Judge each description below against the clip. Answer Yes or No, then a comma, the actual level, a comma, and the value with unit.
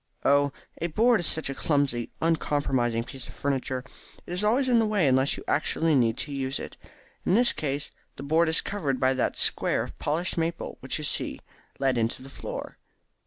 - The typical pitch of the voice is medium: Yes, medium, 145 Hz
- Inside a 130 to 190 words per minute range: No, average, 200 wpm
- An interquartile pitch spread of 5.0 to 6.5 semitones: No, average, 4.3 semitones